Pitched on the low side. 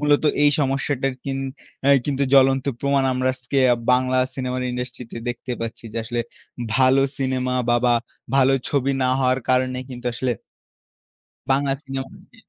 Yes: low, 130 Hz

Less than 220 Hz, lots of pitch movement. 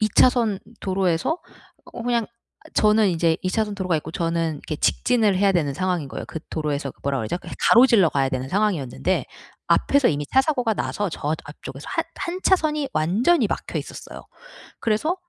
Yes: high, 190 Hz; wide, 6.9 semitones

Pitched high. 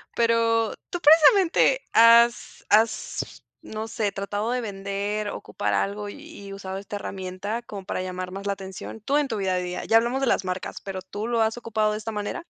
Yes: high, 210 Hz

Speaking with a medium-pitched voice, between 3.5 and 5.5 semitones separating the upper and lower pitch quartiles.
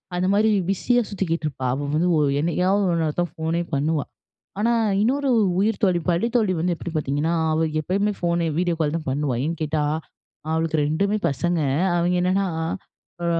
Yes: medium, 170 Hz; average, 3.8 semitones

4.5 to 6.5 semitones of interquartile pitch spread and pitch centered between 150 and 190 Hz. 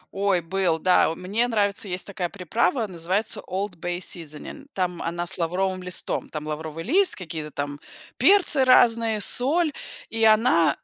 Yes: average, 4.9 semitones; medium, 185 Hz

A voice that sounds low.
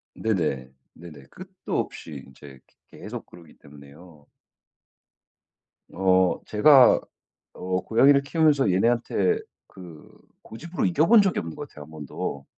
Yes: very low, 95 Hz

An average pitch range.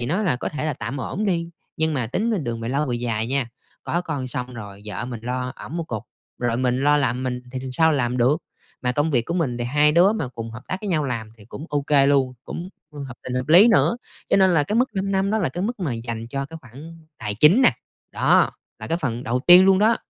No: wide, 5.7 semitones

